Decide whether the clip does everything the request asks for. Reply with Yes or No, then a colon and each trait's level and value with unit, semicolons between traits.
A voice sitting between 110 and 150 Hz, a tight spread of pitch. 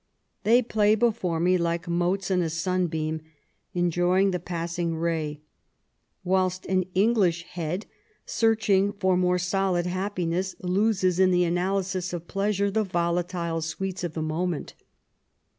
No: medium, 180 Hz; narrow, 2.1 semitones